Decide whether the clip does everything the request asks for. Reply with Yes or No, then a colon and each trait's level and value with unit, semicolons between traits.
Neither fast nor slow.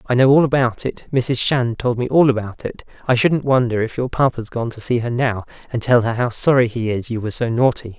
No: fast, 255 wpm